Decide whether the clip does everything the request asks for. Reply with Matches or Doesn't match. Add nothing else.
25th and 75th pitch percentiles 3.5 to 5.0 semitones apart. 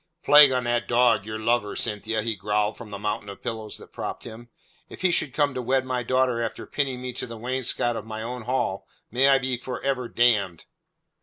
Doesn't match